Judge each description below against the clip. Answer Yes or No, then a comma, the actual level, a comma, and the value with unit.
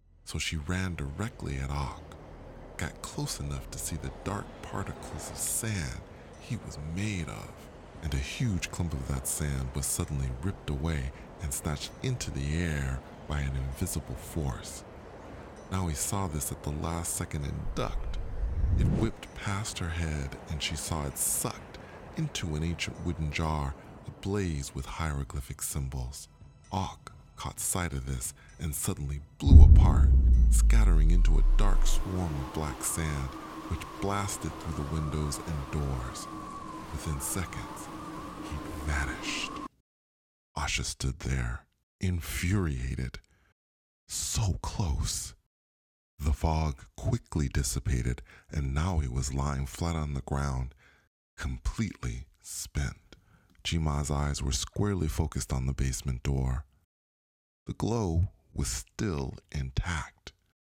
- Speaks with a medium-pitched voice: No, very low, 75 Hz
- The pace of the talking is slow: Yes, slow, 130 wpm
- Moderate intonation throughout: Yes, average, 4.0 semitones